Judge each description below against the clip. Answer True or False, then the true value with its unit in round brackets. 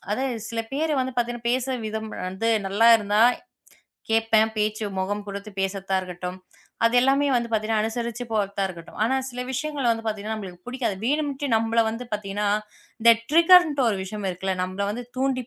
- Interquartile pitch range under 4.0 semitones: True (3.6 semitones)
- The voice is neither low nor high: False (225 Hz)